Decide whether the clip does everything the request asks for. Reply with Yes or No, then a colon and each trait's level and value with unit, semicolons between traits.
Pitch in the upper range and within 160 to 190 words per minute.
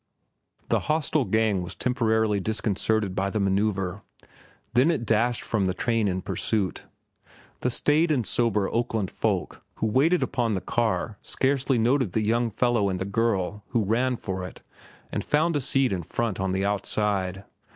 No: low, 110 Hz; average, 165 wpm